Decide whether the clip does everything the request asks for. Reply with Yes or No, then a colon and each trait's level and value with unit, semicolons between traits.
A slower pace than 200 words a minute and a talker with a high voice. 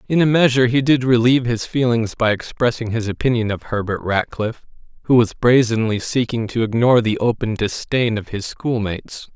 No: average, 175 wpm; low, 115 Hz